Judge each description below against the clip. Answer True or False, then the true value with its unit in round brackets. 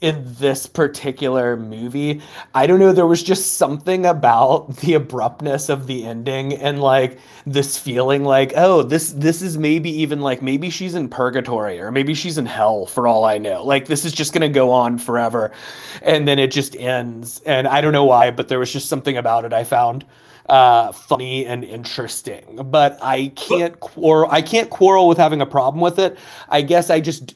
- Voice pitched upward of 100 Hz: True (140 Hz)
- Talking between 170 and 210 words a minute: True (200 wpm)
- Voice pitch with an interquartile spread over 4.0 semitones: False (3.6 semitones)